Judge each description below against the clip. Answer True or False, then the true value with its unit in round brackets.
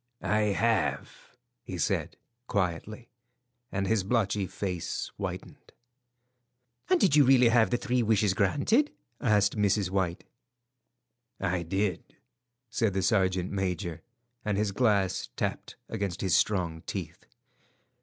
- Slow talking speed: True (120 wpm)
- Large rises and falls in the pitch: False (3.2 semitones)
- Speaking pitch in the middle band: False (100 Hz)